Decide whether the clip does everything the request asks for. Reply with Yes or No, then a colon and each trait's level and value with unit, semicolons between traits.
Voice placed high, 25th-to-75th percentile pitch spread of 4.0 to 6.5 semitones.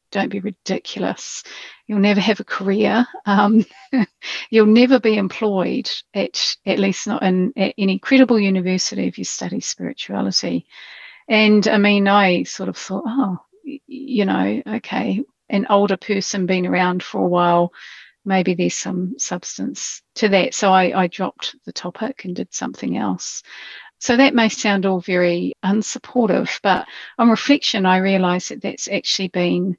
No: high, 200 Hz; average, 3.2 semitones